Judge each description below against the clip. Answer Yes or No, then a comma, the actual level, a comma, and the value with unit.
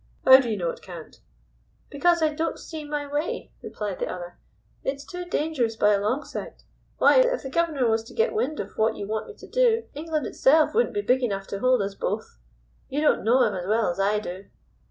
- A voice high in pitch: Yes, very high, 265 Hz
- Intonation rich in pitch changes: Yes, wide, 7.2 semitones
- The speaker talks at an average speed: No, fast, 225 wpm